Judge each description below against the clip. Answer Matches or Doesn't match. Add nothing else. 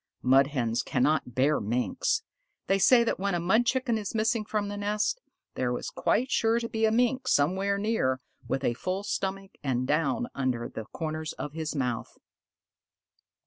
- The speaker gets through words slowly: Doesn't match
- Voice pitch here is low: Doesn't match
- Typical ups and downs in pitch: Doesn't match